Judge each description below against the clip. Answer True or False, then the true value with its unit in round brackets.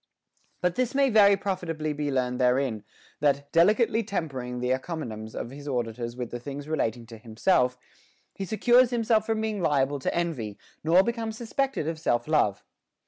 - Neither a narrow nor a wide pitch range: False (8.6 semitones)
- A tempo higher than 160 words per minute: True (170 wpm)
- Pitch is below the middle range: False (150 Hz)